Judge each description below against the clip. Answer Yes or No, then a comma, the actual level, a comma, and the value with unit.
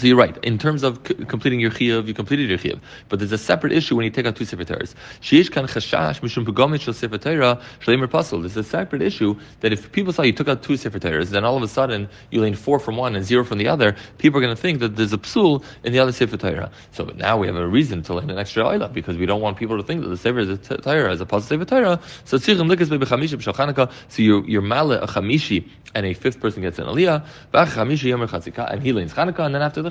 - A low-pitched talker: Yes, low, 120 Hz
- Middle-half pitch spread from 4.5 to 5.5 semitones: Yes, average, 5.1 semitones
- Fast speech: Yes, fast, 235 wpm